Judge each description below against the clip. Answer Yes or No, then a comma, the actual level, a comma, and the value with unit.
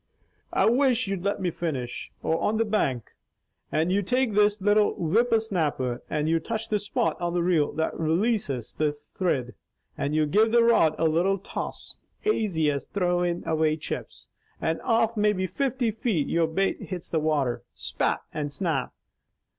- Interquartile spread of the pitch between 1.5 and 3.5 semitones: No, wide, 5.4 semitones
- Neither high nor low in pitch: Yes, medium, 180 Hz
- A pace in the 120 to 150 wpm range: No, average, 170 wpm